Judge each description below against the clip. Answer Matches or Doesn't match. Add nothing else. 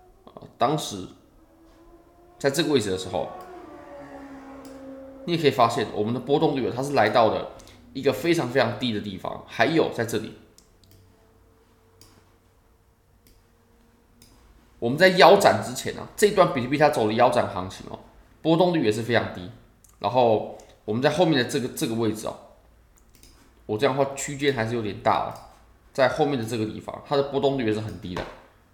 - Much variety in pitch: Matches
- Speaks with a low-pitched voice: Matches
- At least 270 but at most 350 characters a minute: Doesn't match